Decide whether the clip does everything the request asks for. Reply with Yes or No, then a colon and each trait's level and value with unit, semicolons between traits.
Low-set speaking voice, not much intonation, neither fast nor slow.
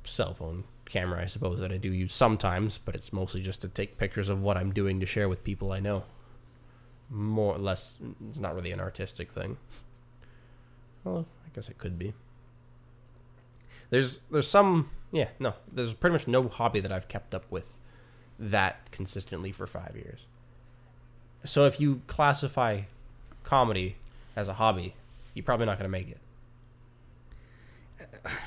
No: low, 120 Hz; average, 4.1 semitones; average, 160 wpm